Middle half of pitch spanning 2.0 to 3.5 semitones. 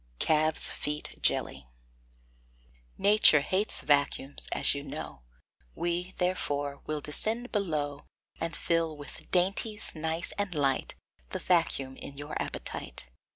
No: average, 4.0 semitones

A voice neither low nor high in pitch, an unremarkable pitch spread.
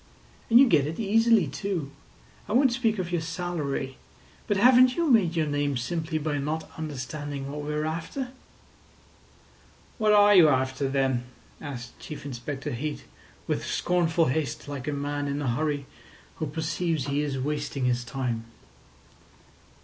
Yes: medium, 150 Hz; average, 4.2 semitones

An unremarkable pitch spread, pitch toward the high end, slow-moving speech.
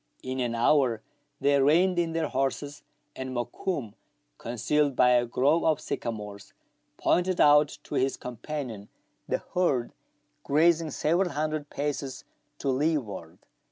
No: average, 4.1 semitones; medium, 140 Hz; slow, 125 wpm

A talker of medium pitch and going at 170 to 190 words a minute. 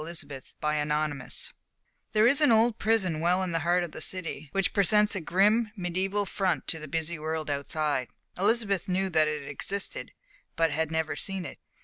Yes: medium, 175 Hz; average, 175 wpm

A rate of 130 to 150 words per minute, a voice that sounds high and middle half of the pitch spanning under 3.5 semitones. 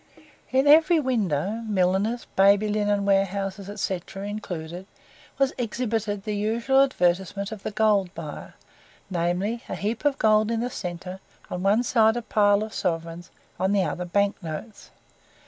Yes: average, 145 wpm; high, 205 Hz; average, 2.9 semitones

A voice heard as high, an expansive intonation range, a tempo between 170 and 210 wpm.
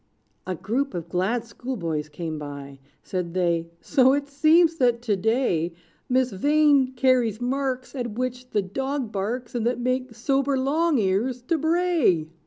No: high, 245 Hz; wide, 6.3 semitones; average, 155 wpm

